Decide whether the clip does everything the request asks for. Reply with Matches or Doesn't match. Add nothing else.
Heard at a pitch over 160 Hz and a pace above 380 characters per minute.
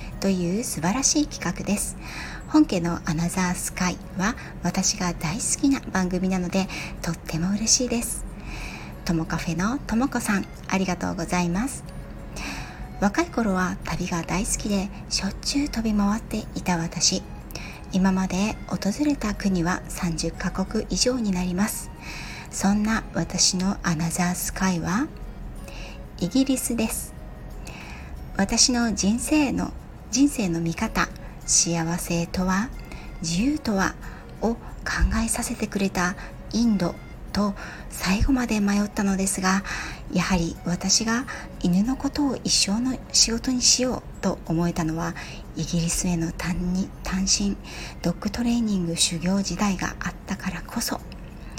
Doesn't match